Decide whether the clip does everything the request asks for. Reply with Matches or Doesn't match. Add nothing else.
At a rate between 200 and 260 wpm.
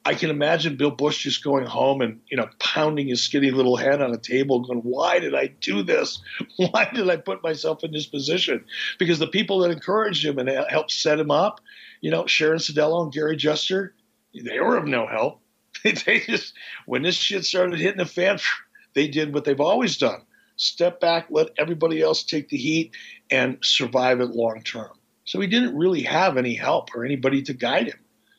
Matches